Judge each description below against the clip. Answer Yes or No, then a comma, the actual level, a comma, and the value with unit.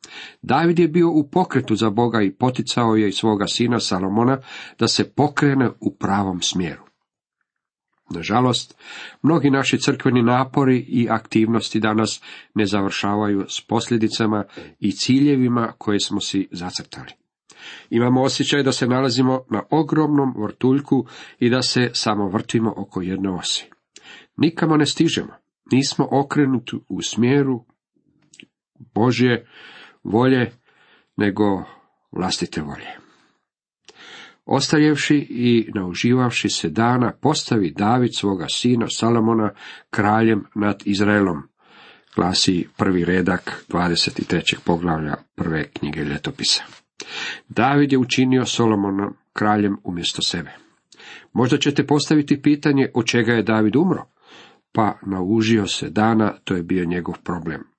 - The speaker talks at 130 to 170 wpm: No, average, 115 wpm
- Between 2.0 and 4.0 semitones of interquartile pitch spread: No, average, 4.4 semitones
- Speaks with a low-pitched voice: Yes, low, 115 Hz